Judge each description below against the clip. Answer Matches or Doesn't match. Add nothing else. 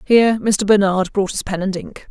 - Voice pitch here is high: Matches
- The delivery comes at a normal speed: Doesn't match